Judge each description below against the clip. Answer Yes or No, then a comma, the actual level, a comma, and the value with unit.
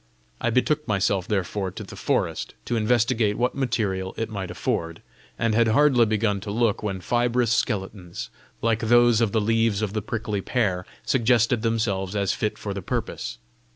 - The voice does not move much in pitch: No, average, 3.1 semitones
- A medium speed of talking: Yes, average, 170 wpm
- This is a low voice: Yes, low, 110 Hz